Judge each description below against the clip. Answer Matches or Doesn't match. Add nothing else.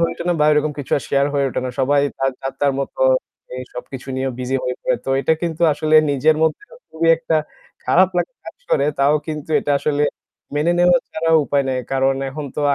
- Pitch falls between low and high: Matches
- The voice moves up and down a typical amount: Matches